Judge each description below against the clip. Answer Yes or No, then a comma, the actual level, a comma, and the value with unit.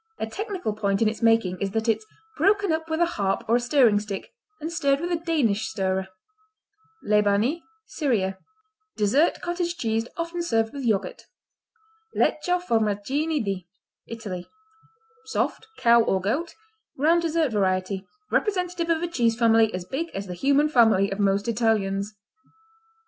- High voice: Yes, high, 230 Hz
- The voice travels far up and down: Yes, wide, 8.0 semitones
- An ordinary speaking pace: Yes, average, 150 wpm